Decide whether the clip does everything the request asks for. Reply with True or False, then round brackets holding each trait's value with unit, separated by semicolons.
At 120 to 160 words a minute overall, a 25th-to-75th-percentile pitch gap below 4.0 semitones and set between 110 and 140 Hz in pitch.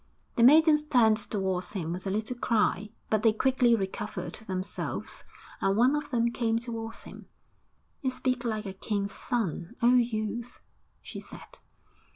False (155 wpm; 3.3 semitones; 225 Hz)